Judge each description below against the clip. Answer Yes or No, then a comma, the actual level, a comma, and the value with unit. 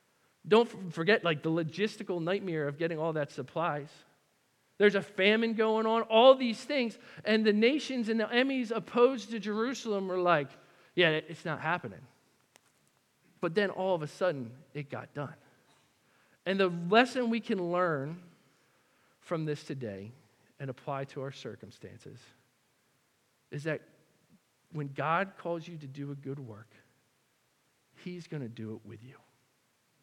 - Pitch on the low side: No, medium, 170 Hz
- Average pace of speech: Yes, average, 150 wpm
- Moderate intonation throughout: No, wide, 7.2 semitones